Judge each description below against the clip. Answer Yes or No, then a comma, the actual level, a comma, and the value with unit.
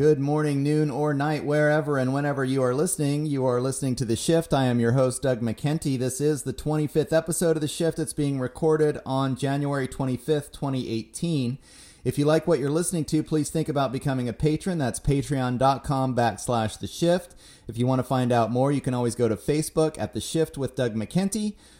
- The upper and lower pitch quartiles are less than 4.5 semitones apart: Yes, average, 3.1 semitones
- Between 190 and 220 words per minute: Yes, fast, 205 wpm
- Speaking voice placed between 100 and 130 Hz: No, medium, 140 Hz